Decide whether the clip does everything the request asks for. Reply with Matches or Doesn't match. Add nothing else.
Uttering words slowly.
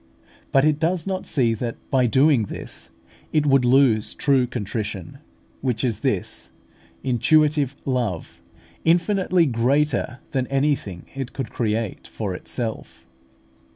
Matches